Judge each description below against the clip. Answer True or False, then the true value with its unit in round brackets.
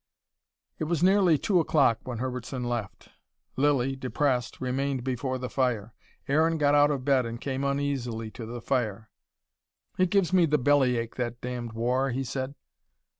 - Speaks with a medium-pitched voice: False (130 Hz)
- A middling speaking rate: True (160 wpm)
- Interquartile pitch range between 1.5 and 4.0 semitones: True (3.0 semitones)